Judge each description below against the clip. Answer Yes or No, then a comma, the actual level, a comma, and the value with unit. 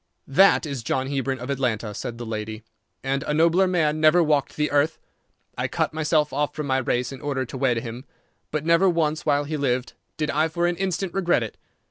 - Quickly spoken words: Yes, fast, 210 wpm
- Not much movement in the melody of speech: No, average, 3.5 semitones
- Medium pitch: Yes, medium, 145 Hz